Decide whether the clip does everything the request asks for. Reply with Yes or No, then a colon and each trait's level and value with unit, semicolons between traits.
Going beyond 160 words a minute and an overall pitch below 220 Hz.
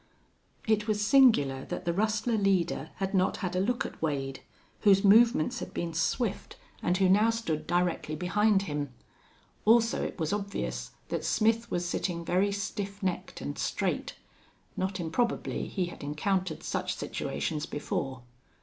No: average, 150 wpm; high, 190 Hz